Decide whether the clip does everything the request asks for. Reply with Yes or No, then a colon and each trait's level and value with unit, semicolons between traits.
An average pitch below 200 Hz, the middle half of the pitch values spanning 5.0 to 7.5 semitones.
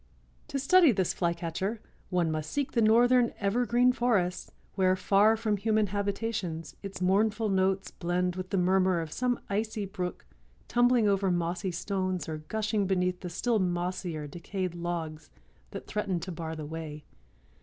No: high, 190 Hz; average, 3.7 semitones